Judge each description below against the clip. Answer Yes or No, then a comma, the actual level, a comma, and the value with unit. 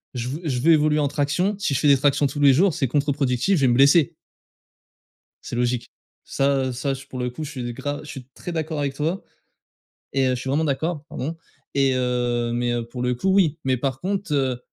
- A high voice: No, medium, 140 Hz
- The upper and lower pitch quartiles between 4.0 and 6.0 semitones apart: No, average, 3.3 semitones